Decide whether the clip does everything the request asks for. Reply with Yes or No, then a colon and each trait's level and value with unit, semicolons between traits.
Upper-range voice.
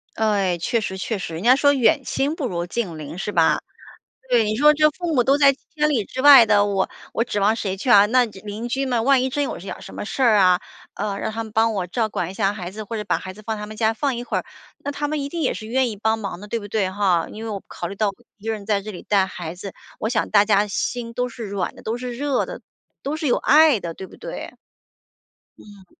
Yes: high, 220 Hz